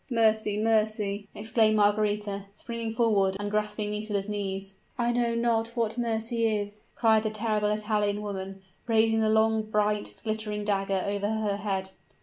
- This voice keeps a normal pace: Yes, average, 145 wpm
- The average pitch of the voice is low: No, high, 210 Hz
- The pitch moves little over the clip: Yes, narrow, 1.4 semitones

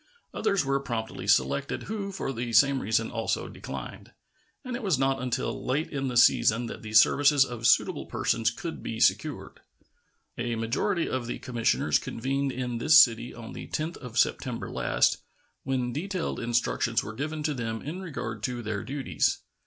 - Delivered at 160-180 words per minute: Yes, average, 170 wpm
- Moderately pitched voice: No, low, 125 Hz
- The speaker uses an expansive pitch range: No, average, 4.1 semitones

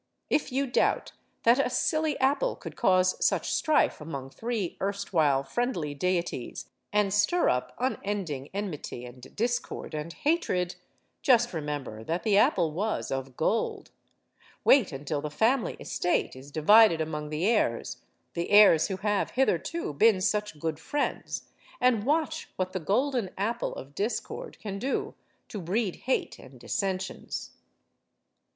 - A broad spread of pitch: Yes, wide, 7.6 semitones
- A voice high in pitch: Yes, high, 195 Hz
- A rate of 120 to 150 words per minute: Yes, average, 140 wpm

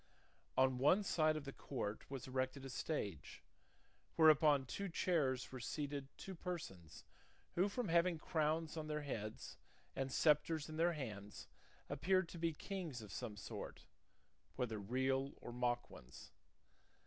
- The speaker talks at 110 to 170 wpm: Yes, average, 150 wpm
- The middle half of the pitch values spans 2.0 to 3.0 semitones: No, average, 4.6 semitones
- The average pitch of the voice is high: No, medium, 140 Hz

